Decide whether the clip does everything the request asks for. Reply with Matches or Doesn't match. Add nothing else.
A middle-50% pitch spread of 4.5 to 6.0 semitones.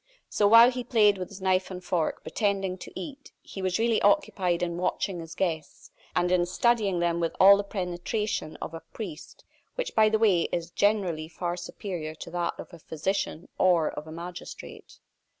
Doesn't match